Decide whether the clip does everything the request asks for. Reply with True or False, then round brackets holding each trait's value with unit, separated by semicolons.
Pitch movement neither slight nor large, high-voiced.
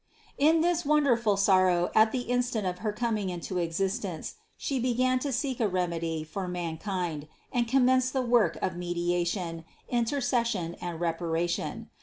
False (6.1 semitones; 200 Hz)